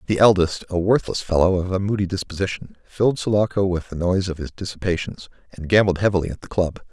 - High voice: No, very low, 95 Hz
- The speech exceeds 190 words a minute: Yes, average, 200 wpm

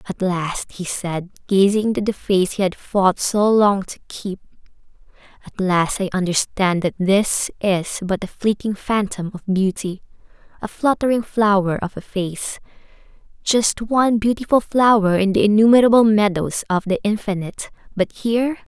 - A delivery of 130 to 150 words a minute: Yes, average, 140 wpm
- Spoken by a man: No, female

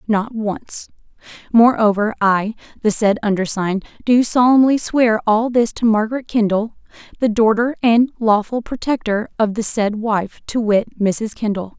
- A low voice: No, high, 220 Hz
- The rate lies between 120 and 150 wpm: Yes, average, 145 wpm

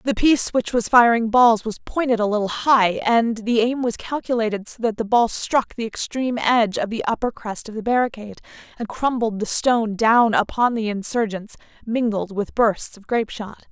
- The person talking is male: No, female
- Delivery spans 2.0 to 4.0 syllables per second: No, 5.2 syllables/s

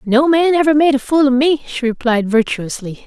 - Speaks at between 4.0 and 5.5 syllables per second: Yes, 5.1 syllables/s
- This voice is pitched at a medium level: No, very high, 265 Hz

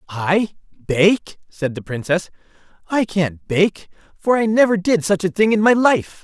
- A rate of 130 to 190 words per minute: Yes, average, 175 wpm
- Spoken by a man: Yes, male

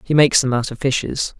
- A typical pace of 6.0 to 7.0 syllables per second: Yes, 6.4 syllables/s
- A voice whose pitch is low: Yes, low, 130 Hz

